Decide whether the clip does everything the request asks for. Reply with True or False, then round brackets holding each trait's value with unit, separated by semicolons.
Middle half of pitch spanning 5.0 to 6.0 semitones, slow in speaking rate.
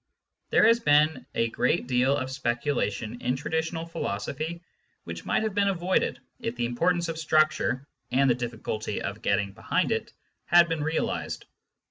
False (5.5 semitones; 155 wpm)